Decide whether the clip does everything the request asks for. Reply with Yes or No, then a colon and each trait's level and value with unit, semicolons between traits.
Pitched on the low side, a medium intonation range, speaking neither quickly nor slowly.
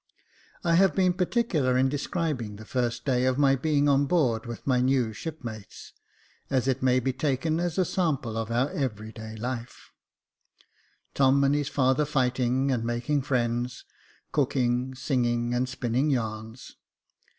Yes: low, 130 Hz; average, 3.2 semitones; average, 160 wpm